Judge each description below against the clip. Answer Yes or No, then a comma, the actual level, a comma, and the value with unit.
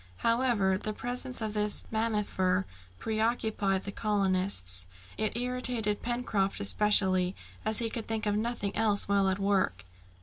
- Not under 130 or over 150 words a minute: Yes, slow, 135 wpm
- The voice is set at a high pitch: Yes, high, 210 Hz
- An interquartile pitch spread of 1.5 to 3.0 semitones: Yes, average, 2.7 semitones